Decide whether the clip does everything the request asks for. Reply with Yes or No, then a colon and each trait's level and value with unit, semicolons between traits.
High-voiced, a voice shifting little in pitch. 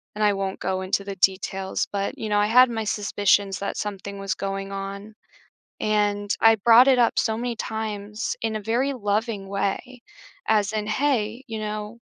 Yes: high, 210 Hz; narrow, 2.0 semitones